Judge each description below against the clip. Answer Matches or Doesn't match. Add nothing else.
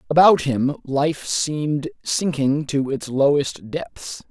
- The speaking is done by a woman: Doesn't match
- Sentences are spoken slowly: Matches